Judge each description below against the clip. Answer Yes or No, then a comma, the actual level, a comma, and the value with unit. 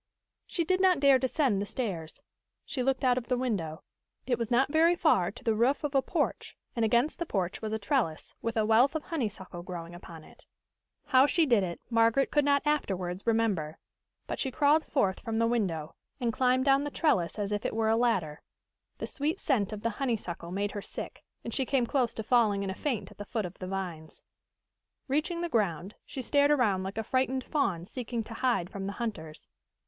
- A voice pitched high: Yes, high, 230 Hz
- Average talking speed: No, fast, 215 wpm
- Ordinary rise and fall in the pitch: No, wide, 5.7 semitones